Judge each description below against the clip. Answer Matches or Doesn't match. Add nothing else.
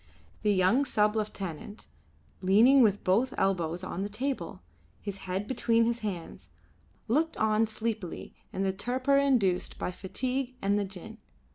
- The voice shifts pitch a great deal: Doesn't match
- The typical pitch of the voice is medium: Doesn't match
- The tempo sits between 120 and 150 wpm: Matches